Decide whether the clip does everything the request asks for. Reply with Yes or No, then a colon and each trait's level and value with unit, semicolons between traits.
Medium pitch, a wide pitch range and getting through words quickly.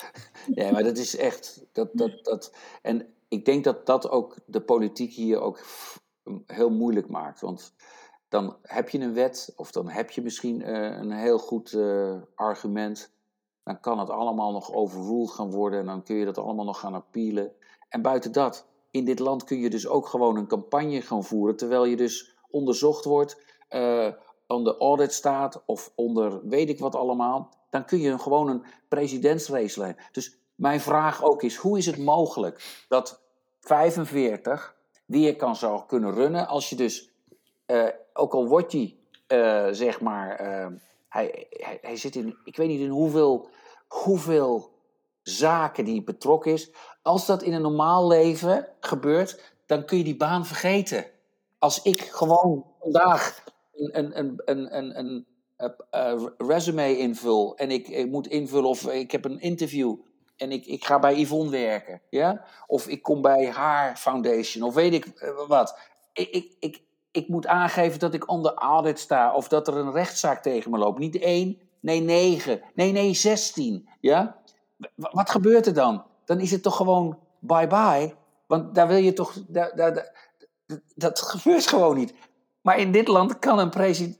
No: medium, 145 Hz; wide, 6.4 semitones; average, 175 wpm